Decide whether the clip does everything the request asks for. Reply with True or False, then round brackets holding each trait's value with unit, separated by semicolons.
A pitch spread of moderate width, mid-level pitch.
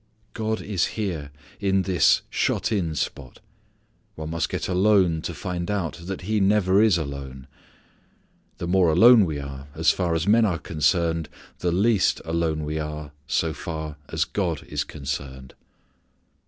False (4.0 semitones; 85 Hz)